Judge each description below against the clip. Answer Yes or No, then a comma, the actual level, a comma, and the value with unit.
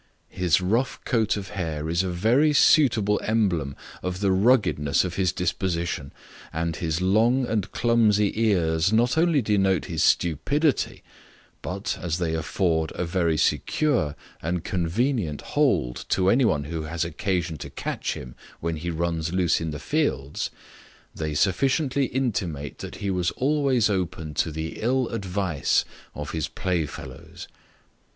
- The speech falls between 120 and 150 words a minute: Yes, average, 145 wpm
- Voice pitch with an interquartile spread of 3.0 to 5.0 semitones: No, wide, 5.5 semitones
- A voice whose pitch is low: Yes, very low, 90 Hz